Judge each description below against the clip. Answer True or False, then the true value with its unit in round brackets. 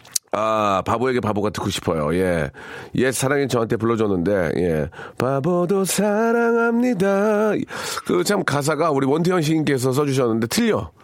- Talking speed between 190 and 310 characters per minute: True (305 characters per minute)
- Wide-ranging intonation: True (8.9 semitones)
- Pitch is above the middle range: False (140 Hz)